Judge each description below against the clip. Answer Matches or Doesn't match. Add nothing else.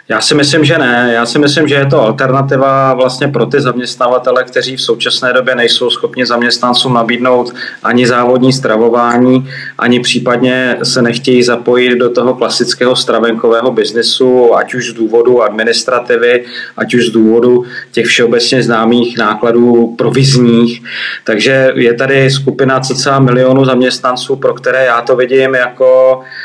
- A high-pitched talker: Doesn't match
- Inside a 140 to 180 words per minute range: Matches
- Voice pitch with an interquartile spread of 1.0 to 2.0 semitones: Matches